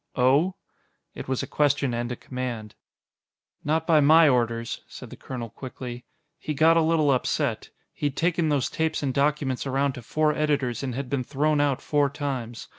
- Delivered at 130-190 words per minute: Yes, average, 180 wpm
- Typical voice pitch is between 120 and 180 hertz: Yes, medium, 140 Hz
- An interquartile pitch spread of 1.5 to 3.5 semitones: Yes, average, 3.2 semitones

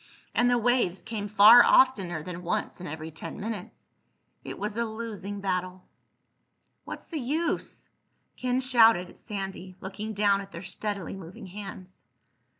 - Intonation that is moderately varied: Yes, average, 3.8 semitones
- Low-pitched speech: No, high, 200 Hz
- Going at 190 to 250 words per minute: No, average, 150 wpm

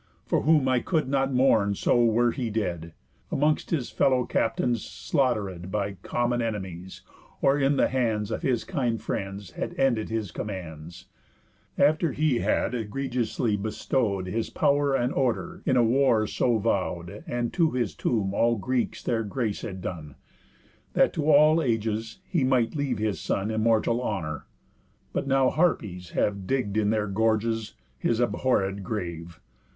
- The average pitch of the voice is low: Yes, low, 115 Hz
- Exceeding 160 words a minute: No, average, 155 wpm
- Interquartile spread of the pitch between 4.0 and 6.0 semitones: Yes, average, 4.5 semitones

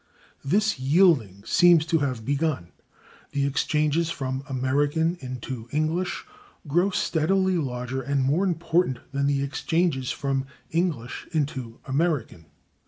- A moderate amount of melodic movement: Yes, average, 4.1 semitones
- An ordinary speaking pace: No, slow, 120 wpm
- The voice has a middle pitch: Yes, medium, 145 Hz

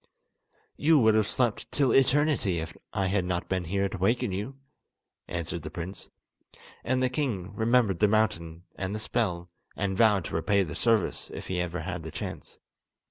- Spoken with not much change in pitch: No, average, 4.7 semitones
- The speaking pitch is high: No, low, 100 Hz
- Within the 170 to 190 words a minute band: Yes, average, 180 wpm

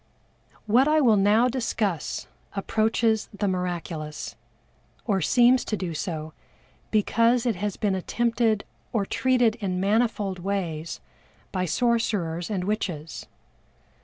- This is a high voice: Yes, high, 205 Hz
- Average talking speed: No, slow, 115 wpm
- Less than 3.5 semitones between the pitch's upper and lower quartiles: No, average, 4.1 semitones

